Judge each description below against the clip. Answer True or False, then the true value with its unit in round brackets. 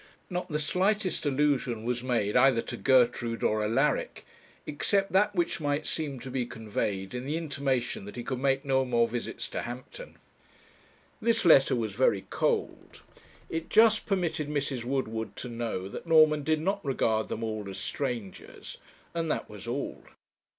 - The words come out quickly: False (165 wpm)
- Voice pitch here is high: False (135 Hz)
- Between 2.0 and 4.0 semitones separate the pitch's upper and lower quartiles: False (5.2 semitones)